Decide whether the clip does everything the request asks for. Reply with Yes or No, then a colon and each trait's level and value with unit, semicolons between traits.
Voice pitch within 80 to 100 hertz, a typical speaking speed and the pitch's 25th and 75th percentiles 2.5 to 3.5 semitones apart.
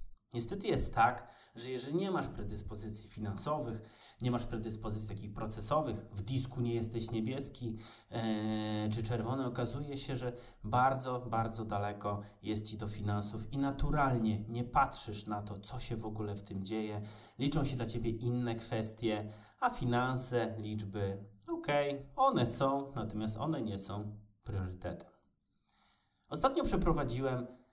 No: low, 115 Hz; average, 140 wpm; average, 3.2 semitones